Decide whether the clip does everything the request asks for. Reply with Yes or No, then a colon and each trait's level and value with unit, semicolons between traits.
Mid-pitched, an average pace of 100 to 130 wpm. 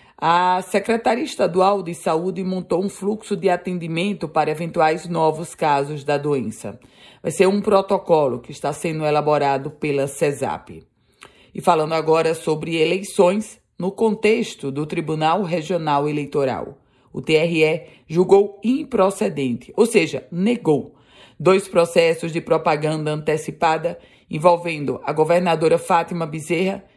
Yes: medium, 165 Hz; slow, 120 wpm